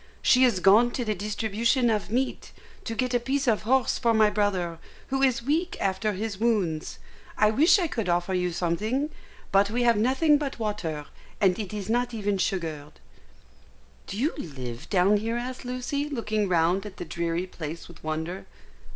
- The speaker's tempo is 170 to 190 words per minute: Yes, average, 180 wpm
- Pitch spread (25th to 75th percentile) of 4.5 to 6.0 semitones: Yes, average, 5.3 semitones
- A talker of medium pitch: No, high, 215 Hz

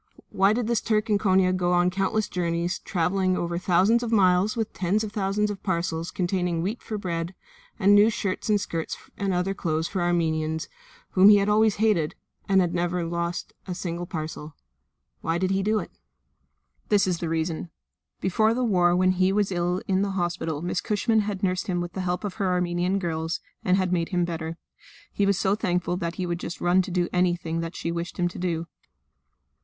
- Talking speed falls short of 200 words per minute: No, fast, 205 wpm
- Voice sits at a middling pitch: Yes, medium, 180 Hz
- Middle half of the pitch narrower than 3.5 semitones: Yes, narrow, 2.5 semitones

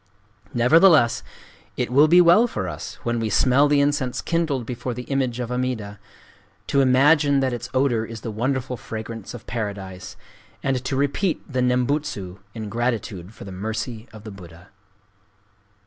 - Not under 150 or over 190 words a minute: Yes, average, 160 wpm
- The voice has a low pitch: Yes, low, 125 Hz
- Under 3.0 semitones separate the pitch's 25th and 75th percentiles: No, average, 4.0 semitones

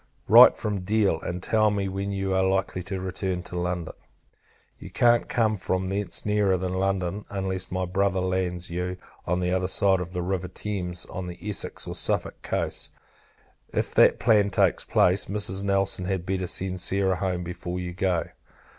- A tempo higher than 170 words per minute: Yes, average, 180 wpm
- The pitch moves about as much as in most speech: No, narrow, 1.5 semitones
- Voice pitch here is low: Yes, very low, 95 Hz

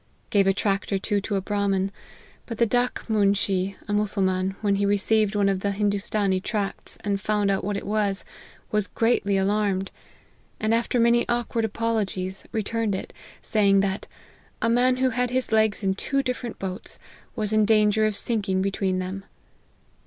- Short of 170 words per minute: No, average, 175 wpm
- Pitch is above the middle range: Yes, high, 205 Hz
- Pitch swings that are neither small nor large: No, narrow, 2.1 semitones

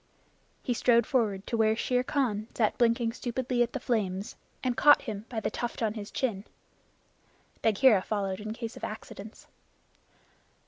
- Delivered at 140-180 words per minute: Yes, average, 155 wpm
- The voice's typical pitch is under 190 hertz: No, high, 225 Hz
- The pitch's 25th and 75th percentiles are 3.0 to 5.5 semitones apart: No, narrow, 2.6 semitones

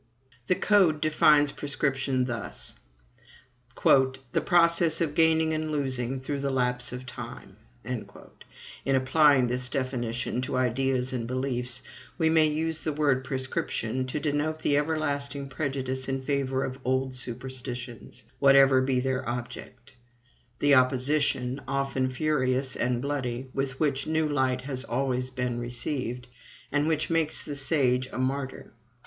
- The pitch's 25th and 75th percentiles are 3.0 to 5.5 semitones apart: No, narrow, 2.4 semitones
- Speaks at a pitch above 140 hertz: No, low, 135 Hz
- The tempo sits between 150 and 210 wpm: No, slow, 135 wpm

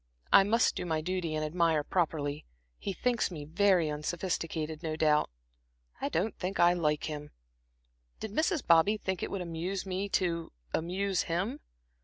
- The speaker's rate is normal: Yes, average, 160 wpm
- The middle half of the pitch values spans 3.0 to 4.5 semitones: Yes, average, 3.5 semitones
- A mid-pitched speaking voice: Yes, medium, 175 Hz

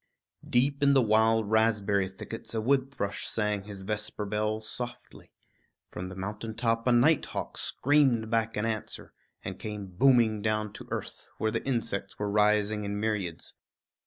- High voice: No, low, 110 Hz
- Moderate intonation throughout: No, narrow, 1.9 semitones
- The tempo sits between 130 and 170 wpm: Yes, average, 160 wpm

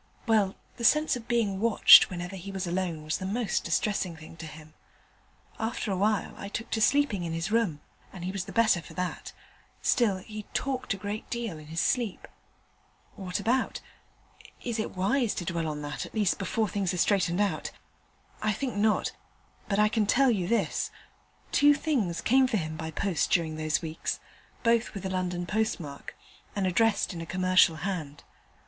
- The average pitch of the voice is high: Yes, high, 195 Hz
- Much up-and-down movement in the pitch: No, average, 4.4 semitones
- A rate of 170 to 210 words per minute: Yes, average, 185 wpm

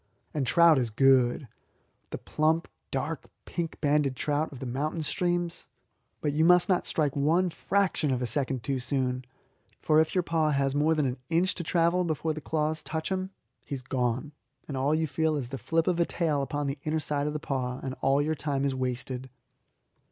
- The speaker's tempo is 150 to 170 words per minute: No, fast, 205 wpm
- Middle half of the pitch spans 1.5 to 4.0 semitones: Yes, average, 3.3 semitones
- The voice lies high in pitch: No, medium, 150 Hz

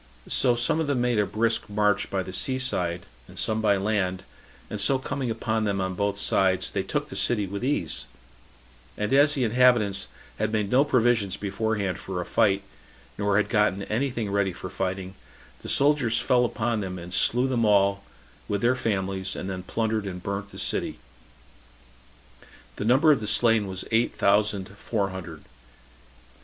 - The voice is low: Yes, low, 105 Hz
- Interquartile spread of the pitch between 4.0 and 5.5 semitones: No, average, 3.6 semitones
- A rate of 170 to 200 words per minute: Yes, average, 180 wpm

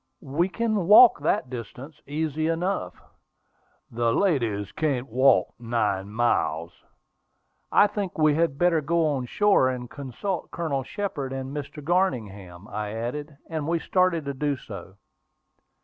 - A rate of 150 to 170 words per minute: No, slow, 135 wpm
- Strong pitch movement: Yes, wide, 5.9 semitones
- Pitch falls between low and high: Yes, medium, 145 Hz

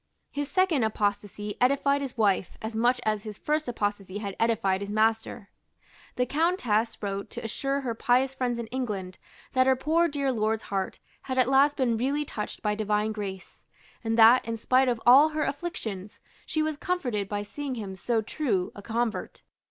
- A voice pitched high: Yes, high, 230 Hz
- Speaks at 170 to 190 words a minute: Yes, average, 180 wpm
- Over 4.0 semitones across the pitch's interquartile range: Yes, average, 4.5 semitones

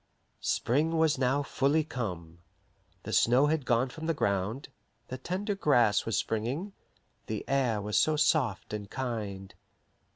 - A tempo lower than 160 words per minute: Yes, average, 140 wpm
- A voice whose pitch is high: No, low, 130 Hz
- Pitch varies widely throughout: Yes, wide, 6.1 semitones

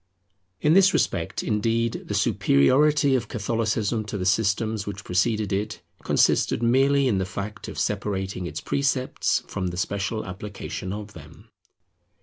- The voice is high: No, low, 105 Hz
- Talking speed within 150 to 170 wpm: No, average, 140 wpm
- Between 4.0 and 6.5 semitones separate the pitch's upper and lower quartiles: No, average, 3.3 semitones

